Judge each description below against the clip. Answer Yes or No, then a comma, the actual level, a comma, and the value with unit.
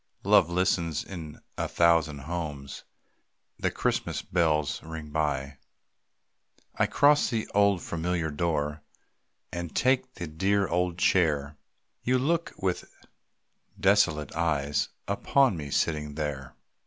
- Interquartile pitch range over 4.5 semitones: No, average, 4.1 semitones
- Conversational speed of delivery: No, slow, 115 wpm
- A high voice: No, very low, 85 Hz